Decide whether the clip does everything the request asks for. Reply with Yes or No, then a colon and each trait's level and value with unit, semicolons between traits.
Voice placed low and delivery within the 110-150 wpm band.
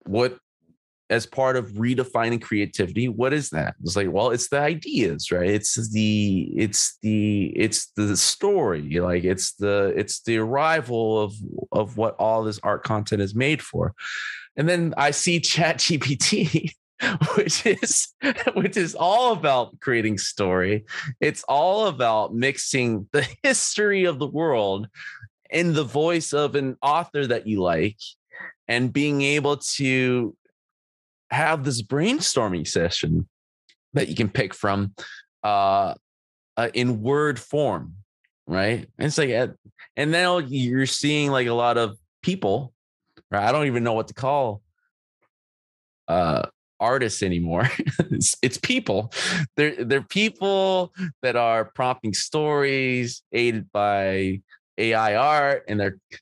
Yes: low, 125 Hz; average, 140 wpm